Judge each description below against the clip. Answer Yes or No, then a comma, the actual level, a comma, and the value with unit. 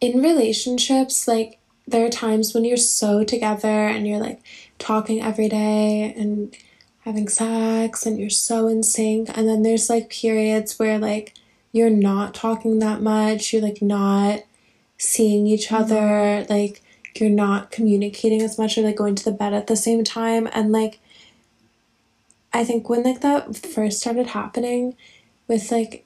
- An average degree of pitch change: No, narrow, 1.4 semitones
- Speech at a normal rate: Yes, average, 160 wpm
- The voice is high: Yes, high, 220 Hz